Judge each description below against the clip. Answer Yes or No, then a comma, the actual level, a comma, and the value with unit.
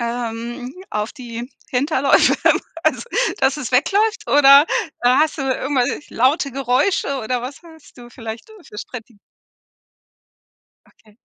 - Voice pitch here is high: Yes, very high, 255 Hz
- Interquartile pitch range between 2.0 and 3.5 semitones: Yes, average, 2.9 semitones